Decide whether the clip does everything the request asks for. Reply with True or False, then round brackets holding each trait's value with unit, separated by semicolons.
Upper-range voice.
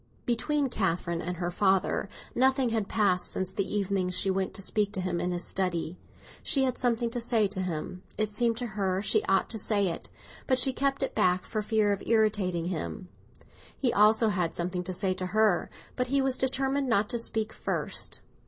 True (205 Hz)